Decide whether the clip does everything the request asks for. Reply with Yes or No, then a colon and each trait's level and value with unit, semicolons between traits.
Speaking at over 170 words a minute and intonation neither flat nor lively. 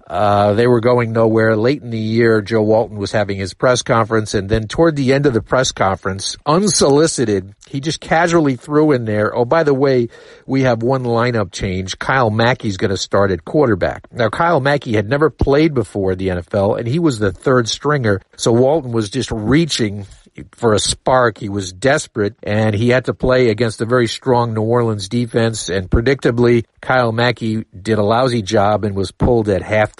Yes: average, 200 wpm; average, 3.4 semitones